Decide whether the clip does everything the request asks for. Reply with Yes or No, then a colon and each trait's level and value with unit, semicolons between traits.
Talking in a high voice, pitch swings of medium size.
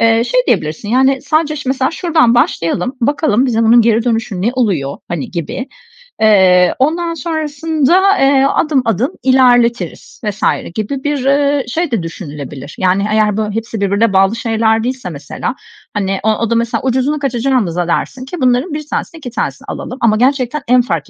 Yes: high, 240 Hz; average, 4.9 semitones